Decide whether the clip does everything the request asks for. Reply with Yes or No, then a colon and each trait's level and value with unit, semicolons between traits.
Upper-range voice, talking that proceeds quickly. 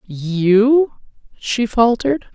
No: high, 230 Hz; slow, 75 wpm